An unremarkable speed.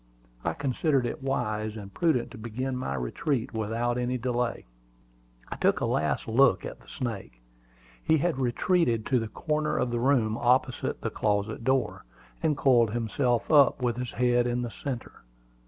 Yes: average, 170 wpm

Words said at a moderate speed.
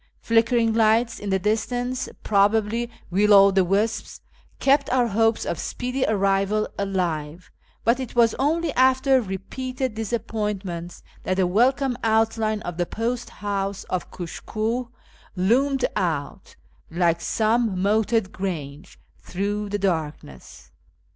No: slow, 125 wpm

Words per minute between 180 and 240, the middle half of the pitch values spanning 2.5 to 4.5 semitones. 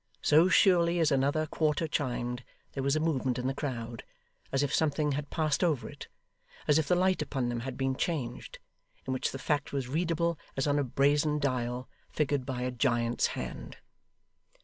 Yes: average, 185 wpm; average, 3.3 semitones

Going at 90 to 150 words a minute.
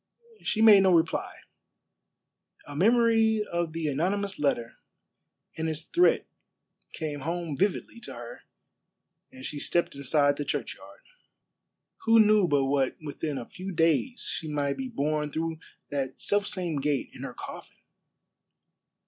Yes: average, 140 wpm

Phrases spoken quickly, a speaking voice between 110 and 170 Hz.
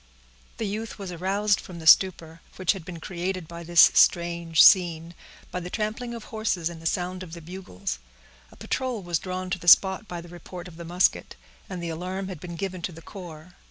No: fast, 210 wpm; medium, 180 Hz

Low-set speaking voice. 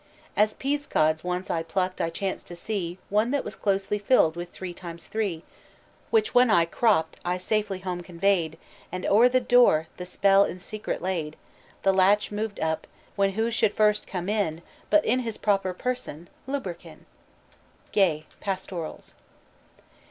No: high, 195 Hz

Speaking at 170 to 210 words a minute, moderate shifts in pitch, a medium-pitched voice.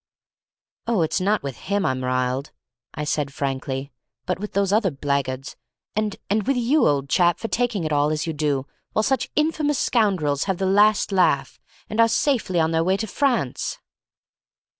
No: average, 175 wpm; wide, 7.2 semitones; medium, 180 Hz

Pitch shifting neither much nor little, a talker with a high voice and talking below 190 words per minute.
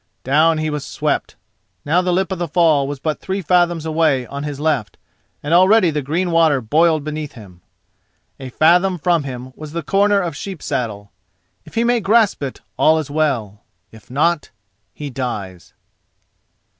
No: average, 4.1 semitones; medium, 155 Hz; average, 170 wpm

